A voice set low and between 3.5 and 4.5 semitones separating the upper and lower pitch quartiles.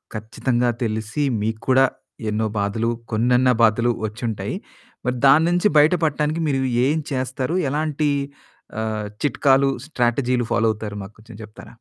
Yes: low, 125 Hz; average, 4.0 semitones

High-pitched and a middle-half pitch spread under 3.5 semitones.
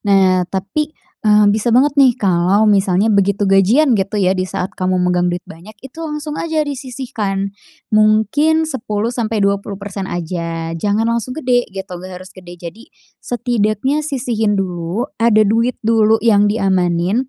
No: high, 210 Hz; average, 4.3 semitones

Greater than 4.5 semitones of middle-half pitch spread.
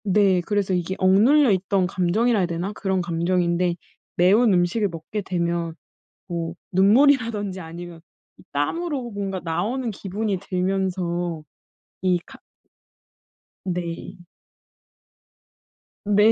No: average, 3.1 semitones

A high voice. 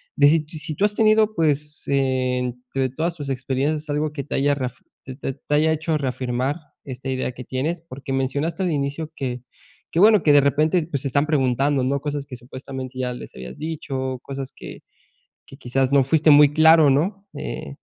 No: medium, 140 Hz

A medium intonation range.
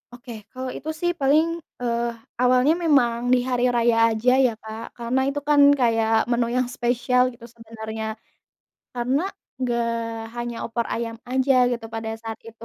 No: narrow, 1.8 semitones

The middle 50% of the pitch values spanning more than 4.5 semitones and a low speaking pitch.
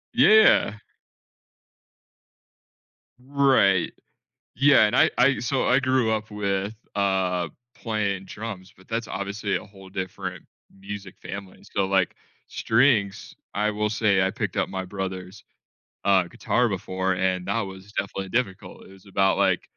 No: average, 2.7 semitones; low, 100 Hz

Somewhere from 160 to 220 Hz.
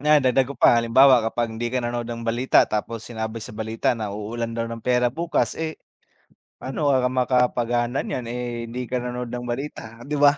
No: low, 120 Hz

